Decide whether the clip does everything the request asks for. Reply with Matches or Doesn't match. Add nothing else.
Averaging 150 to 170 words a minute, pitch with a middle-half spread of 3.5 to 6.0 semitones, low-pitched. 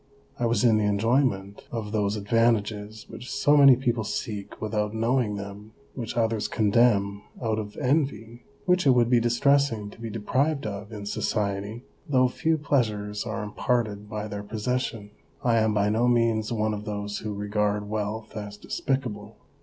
Doesn't match